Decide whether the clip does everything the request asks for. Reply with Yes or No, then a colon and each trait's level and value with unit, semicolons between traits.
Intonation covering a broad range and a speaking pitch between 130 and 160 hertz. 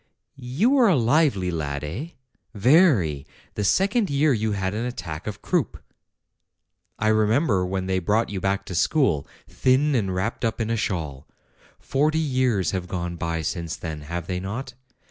No: wide, 6.8 semitones; low, 105 Hz